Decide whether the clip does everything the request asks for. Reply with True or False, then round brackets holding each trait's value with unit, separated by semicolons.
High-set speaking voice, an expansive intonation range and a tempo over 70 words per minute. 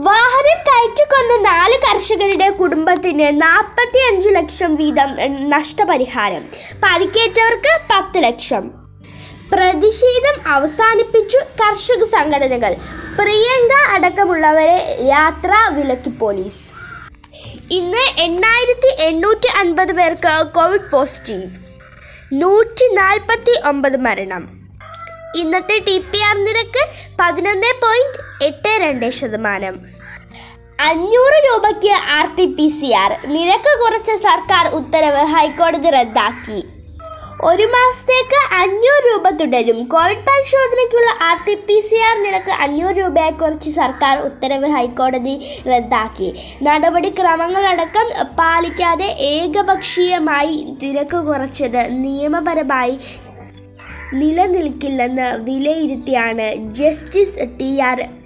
True (335 Hz; 6.7 semitones; 85 wpm)